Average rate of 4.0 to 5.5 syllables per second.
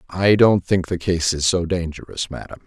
Yes: 4.9 syllables/s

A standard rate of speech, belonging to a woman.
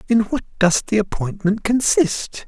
No: average, 145 wpm; male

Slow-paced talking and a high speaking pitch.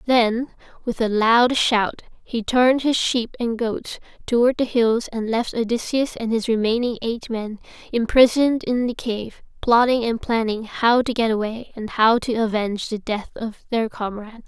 No: average, 175 wpm; high, 230 Hz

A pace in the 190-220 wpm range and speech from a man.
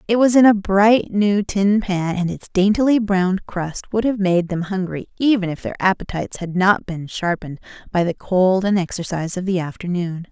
No: average, 200 wpm; female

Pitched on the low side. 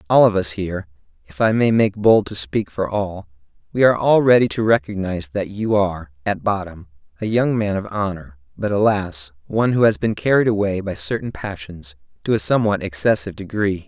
Yes: low, 100 Hz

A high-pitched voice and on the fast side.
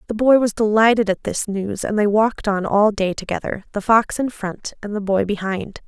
Yes: high, 210 Hz; fast, 225 wpm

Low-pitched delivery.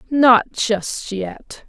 No: high, 225 Hz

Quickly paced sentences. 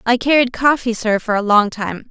Yes: fast, 230 wpm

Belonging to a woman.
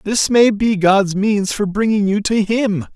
No: male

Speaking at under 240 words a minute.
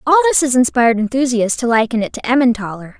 Yes: average, 200 wpm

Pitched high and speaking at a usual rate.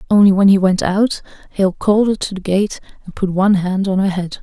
No: high, 195 Hz; fast, 245 wpm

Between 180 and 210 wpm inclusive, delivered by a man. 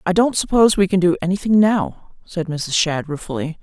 No: average, 200 wpm; female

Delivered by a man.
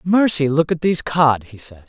Yes: male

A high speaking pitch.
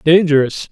No: medium, 155 Hz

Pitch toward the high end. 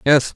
No: medium, 140 Hz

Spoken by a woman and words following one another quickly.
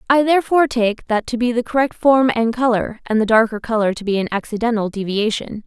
Yes: female; fast, 210 wpm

